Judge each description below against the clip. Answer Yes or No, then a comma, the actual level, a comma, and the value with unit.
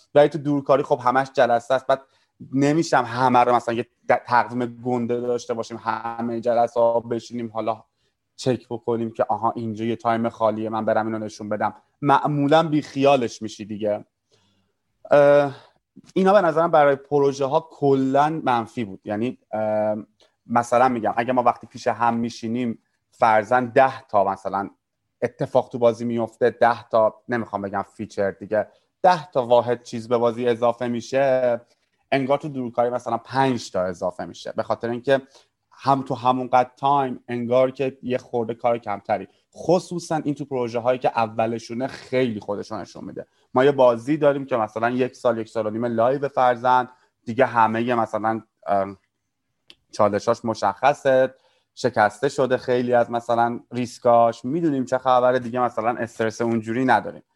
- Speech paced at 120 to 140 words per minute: No, fast, 155 wpm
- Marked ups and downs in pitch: No, narrow, 2.6 semitones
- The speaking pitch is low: Yes, low, 120 Hz